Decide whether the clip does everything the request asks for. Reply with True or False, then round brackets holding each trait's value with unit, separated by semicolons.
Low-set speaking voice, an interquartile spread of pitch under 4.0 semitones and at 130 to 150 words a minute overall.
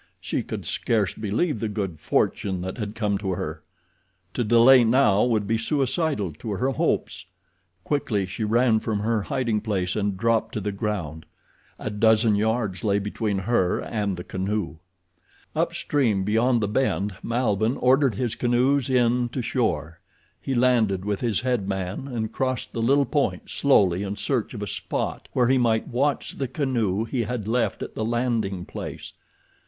False (110 Hz; 3.5 semitones; 170 wpm)